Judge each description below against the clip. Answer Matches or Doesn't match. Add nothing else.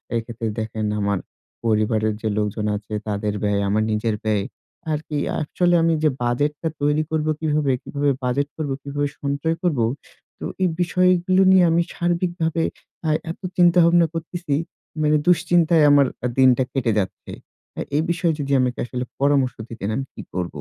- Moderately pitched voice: Matches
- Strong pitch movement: Matches